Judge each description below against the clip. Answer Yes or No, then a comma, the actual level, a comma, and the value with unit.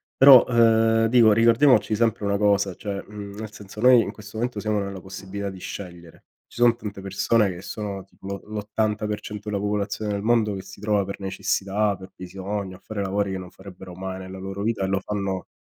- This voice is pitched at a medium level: No, low, 100 Hz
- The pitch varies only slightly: Yes, narrow, 2.0 semitones